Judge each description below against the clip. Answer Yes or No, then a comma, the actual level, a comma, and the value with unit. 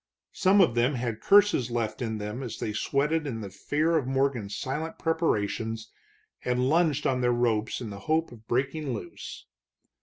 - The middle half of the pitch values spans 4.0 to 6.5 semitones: Yes, average, 5.2 semitones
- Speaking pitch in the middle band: No, low, 125 Hz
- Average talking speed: Yes, average, 175 wpm